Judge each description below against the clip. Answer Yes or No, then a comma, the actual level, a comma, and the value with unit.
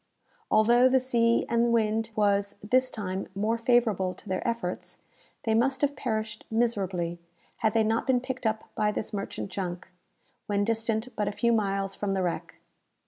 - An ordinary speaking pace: Yes, average, 170 wpm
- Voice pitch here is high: Yes, high, 220 Hz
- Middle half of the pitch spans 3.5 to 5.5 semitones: No, average, 2.8 semitones